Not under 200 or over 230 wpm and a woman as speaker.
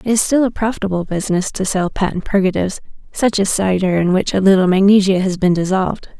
Yes: fast, 205 wpm; female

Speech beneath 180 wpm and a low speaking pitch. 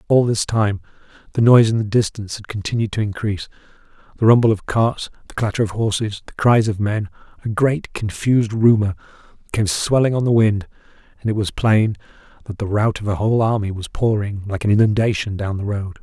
No: average, 195 wpm; low, 105 Hz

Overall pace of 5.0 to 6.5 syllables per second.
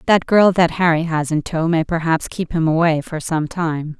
No: 4.7 syllables/s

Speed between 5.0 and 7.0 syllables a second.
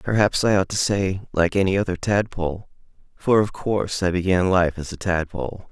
Yes: 5.3 syllables/s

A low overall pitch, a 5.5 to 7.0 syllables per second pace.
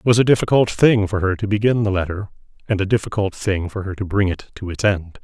Yes: low, 100 Hz; 6.0 syllables/s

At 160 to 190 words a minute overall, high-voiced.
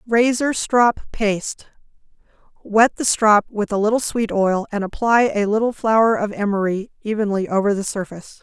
No: average, 150 wpm; high, 210 Hz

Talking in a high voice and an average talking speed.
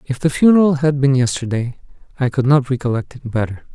No: low, 135 Hz; average, 190 wpm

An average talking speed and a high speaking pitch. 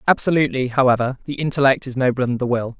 No: average, 195 wpm; low, 130 Hz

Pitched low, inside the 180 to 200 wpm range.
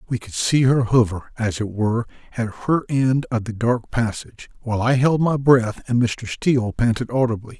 Yes: low, 120 Hz; average, 195 wpm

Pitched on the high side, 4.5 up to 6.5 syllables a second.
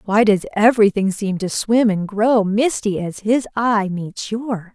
No: high, 210 Hz; 4.1 syllables/s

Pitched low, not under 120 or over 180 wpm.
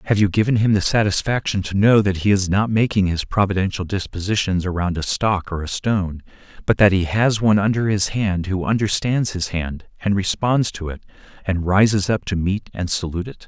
No: low, 100 Hz; fast, 205 wpm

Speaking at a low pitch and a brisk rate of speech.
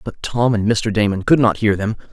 Yes: low, 110 Hz; fast, 255 wpm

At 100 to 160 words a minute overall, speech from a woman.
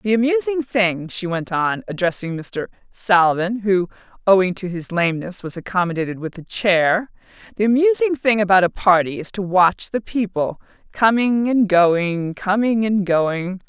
Yes: average, 155 wpm; female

